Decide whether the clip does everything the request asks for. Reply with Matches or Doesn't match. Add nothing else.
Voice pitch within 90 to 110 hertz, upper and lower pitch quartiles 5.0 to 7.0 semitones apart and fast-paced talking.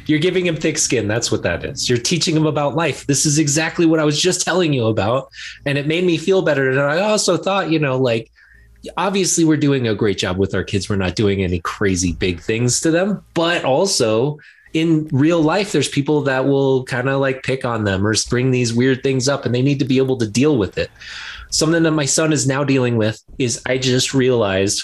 Doesn't match